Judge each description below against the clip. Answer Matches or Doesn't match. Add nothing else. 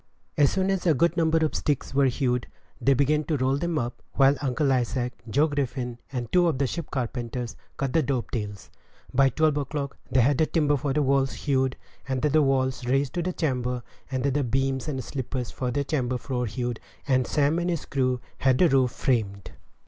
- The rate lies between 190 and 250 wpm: Matches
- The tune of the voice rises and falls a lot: Doesn't match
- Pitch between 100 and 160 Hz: Matches